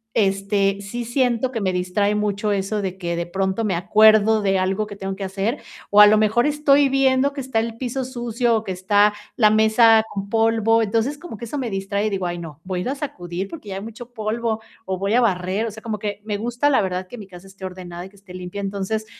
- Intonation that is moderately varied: Yes, average, 3.0 semitones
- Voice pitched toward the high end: Yes, high, 210 Hz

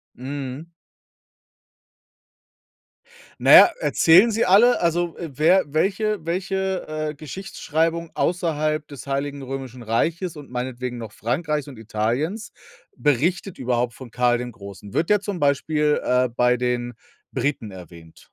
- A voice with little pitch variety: No, wide, 5.5 semitones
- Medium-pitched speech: Yes, medium, 145 Hz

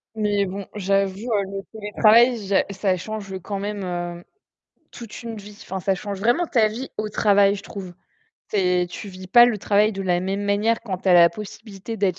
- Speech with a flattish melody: Yes, narrow, 2.1 semitones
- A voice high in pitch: Yes, high, 200 Hz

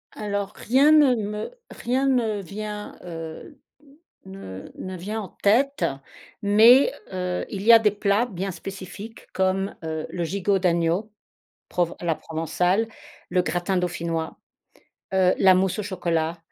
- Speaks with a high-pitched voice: Yes, high, 195 Hz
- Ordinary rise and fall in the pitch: Yes, average, 3.4 semitones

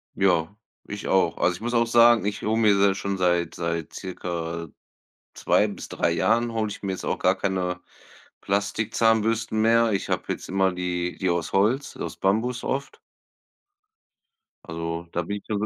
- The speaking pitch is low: Yes, low, 100 Hz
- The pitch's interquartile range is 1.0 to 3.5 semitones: No, average, 3.9 semitones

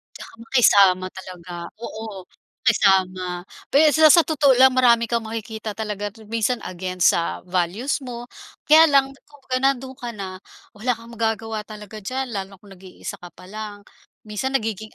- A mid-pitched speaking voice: No, high, 220 Hz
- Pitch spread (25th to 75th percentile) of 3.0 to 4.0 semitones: No, average, 4.5 semitones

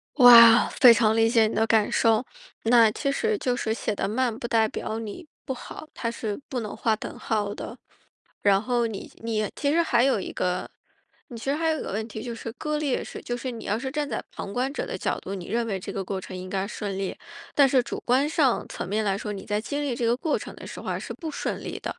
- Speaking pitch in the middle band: No, high, 230 Hz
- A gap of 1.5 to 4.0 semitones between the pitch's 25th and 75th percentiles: Yes, average, 3.6 semitones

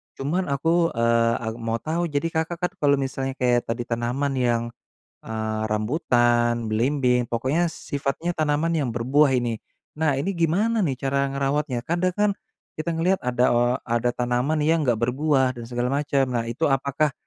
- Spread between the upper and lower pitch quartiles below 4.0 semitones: No, average, 4.6 semitones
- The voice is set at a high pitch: No, low, 135 Hz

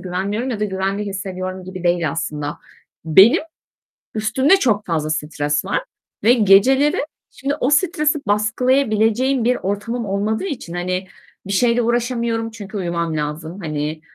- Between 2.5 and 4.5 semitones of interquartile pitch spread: No, average, 5.2 semitones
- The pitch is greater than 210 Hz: No, high, 205 Hz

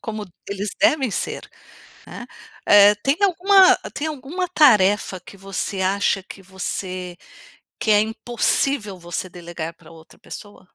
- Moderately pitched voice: No, high, 205 Hz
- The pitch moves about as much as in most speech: No, wide, 6.2 semitones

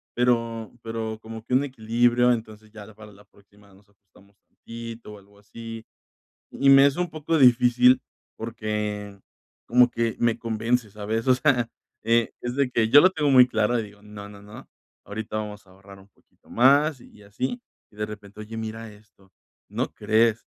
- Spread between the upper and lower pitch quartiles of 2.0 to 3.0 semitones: Yes, average, 2.7 semitones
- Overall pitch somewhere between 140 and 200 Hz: No, low, 115 Hz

